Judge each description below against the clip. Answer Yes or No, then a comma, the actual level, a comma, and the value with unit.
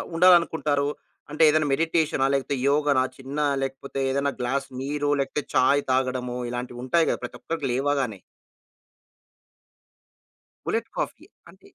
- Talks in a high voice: No, medium, 140 Hz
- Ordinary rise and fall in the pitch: No, narrow, 2.3 semitones